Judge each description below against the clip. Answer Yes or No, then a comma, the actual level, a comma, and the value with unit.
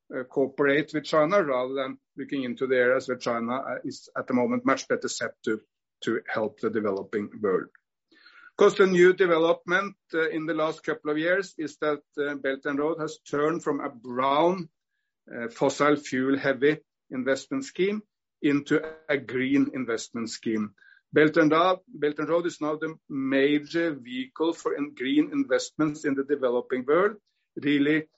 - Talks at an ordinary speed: Yes, average, 170 wpm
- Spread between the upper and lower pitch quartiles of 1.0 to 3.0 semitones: No, average, 4.0 semitones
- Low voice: No, medium, 150 Hz